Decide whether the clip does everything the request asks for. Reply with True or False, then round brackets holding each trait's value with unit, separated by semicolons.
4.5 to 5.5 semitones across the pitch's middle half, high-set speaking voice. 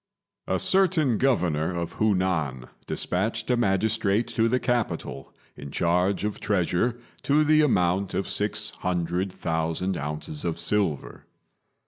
False (4.9 semitones; 95 Hz)